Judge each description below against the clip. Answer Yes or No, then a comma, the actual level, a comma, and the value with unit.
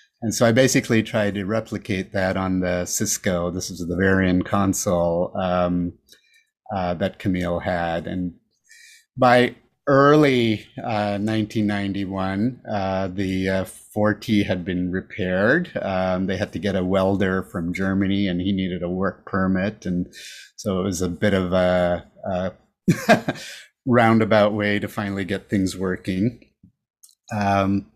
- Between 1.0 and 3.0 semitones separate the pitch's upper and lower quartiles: Yes, average, 2.7 semitones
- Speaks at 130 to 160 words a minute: Yes, average, 140 wpm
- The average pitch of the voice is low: Yes, very low, 95 Hz